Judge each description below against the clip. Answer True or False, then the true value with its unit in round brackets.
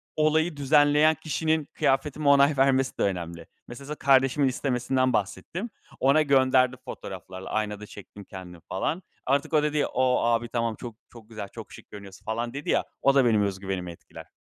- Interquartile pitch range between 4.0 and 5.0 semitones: False (5.4 semitones)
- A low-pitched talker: True (130 Hz)